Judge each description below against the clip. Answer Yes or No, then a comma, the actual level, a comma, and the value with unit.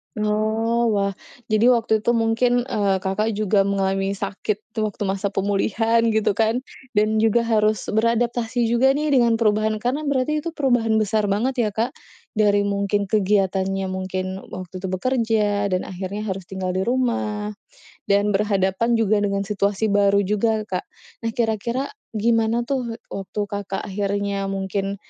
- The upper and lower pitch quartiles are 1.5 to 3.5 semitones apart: Yes, narrow, 2.5 semitones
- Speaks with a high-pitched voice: Yes, high, 210 Hz